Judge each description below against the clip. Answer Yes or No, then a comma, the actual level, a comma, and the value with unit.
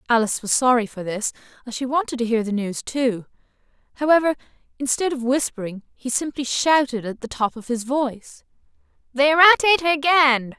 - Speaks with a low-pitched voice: No, very high, 260 Hz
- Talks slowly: No, average, 170 wpm